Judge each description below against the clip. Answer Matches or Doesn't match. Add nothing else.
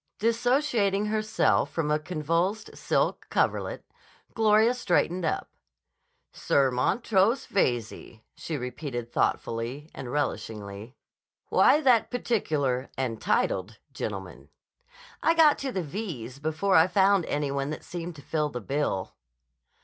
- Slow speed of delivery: Matches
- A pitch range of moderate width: Doesn't match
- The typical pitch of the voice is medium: Matches